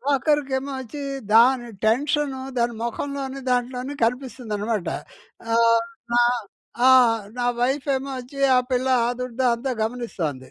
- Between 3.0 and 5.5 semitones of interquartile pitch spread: No, narrow, 2.5 semitones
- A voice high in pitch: Yes, very high, 250 Hz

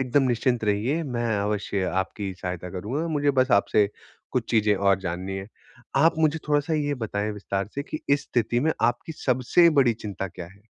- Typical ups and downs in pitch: No, wide, 6.1 semitones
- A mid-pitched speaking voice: No, low, 115 Hz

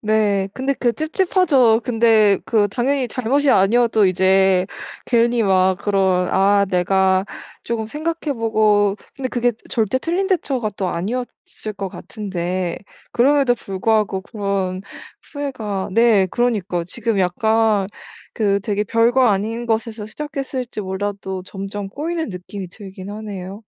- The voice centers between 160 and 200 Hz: No, high, 215 Hz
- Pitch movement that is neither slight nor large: Yes, average, 4.0 semitones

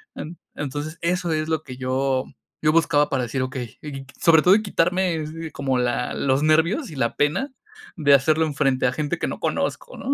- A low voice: No, medium, 150 Hz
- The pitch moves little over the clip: No, average, 3.5 semitones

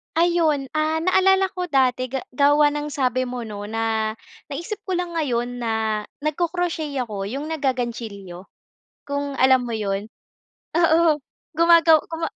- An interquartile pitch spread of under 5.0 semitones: No, wide, 5.6 semitones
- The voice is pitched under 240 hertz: No, very high, 280 Hz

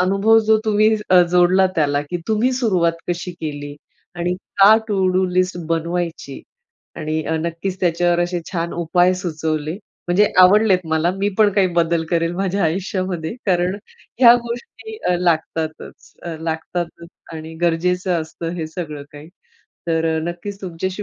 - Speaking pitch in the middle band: Yes, medium, 175 Hz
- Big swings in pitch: No, average, 2.7 semitones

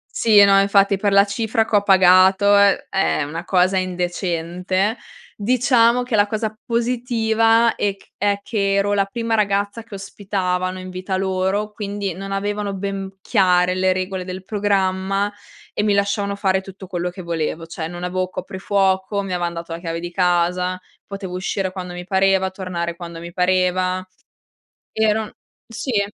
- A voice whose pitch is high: Yes, high, 195 Hz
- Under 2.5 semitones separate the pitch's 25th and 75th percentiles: Yes, narrow, 1.9 semitones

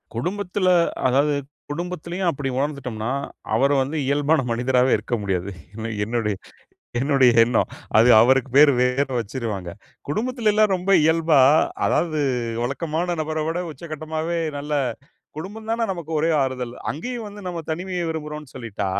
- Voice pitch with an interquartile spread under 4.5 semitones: No, wide, 5.4 semitones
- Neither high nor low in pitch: Yes, medium, 150 Hz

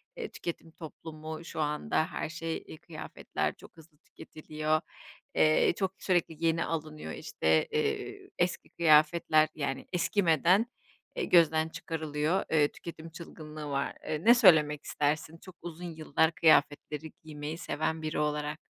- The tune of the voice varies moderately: No, narrow, 1.7 semitones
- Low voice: No, medium, 160 Hz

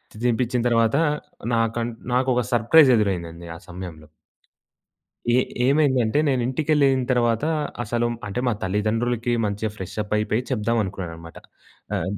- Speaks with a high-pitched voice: No, low, 115 Hz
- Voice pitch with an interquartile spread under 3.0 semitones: No, average, 3.5 semitones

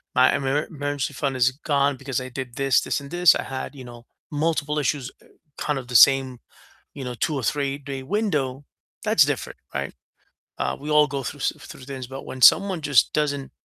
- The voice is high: No, medium, 140 Hz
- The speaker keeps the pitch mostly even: Yes, narrow, 2.1 semitones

